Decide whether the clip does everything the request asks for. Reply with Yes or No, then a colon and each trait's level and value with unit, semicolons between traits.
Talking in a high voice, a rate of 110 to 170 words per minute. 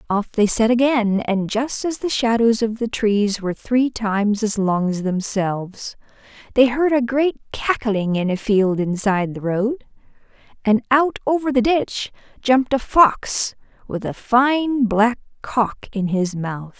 Yes: high, 225 Hz; average, 165 wpm